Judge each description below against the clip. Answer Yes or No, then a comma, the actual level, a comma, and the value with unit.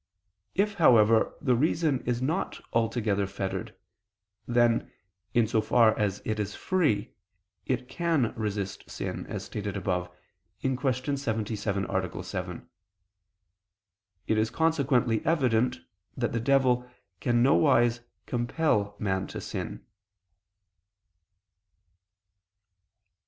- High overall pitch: No, low, 115 Hz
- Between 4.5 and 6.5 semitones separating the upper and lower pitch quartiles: No, average, 4.1 semitones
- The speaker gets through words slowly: Yes, slow, 105 wpm